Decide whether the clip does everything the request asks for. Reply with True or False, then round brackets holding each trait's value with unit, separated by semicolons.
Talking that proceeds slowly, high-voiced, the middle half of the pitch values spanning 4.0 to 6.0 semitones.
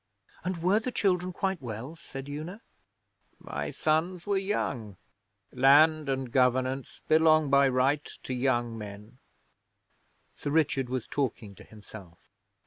False (130 wpm; 140 Hz; 4.6 semitones)